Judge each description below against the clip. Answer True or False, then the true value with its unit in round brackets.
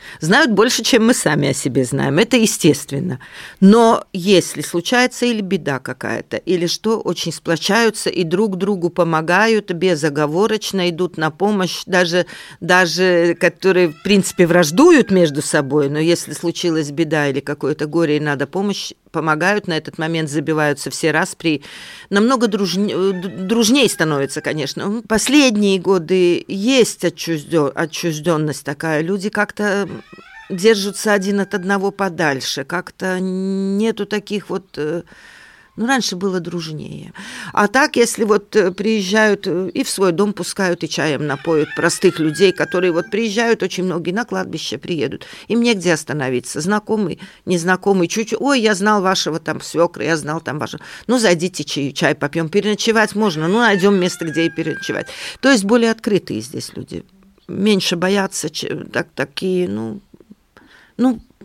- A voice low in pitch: False (185 Hz)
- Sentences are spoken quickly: False (140 wpm)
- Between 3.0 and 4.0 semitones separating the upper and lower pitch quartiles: False (4.5 semitones)